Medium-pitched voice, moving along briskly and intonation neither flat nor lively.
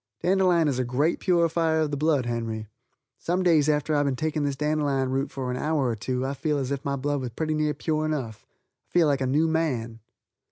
Yes: medium, 145 Hz; fast, 230 wpm; average, 3.3 semitones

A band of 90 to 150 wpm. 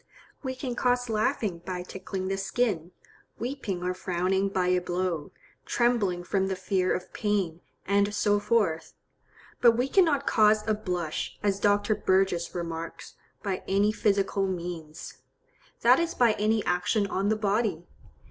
Yes: average, 145 wpm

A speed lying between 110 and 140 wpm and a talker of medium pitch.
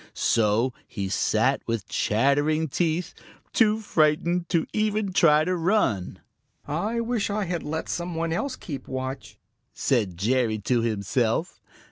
Yes: slow, 135 wpm; medium, 155 Hz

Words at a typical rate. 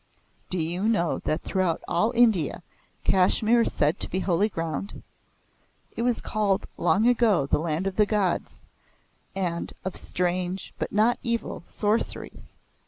Yes: average, 145 wpm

